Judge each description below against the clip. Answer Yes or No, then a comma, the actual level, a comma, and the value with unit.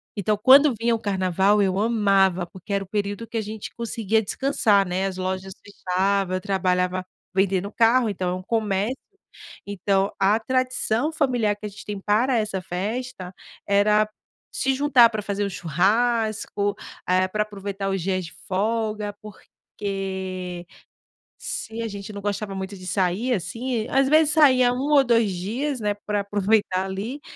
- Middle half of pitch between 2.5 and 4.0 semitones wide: Yes, average, 3.2 semitones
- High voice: Yes, high, 205 Hz